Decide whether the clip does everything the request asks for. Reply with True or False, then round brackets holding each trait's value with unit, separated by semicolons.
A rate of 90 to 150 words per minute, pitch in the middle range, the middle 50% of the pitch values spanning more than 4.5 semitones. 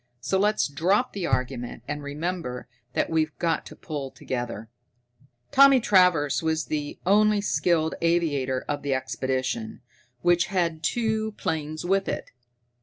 True (140 wpm; 160 Hz; 5.2 semitones)